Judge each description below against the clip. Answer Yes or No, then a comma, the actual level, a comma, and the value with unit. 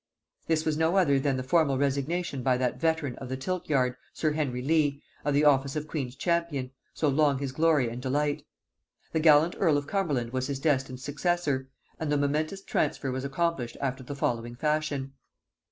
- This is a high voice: No, medium, 145 Hz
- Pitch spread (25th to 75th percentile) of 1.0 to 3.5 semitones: Yes, average, 3.0 semitones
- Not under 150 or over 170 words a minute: No, average, 185 wpm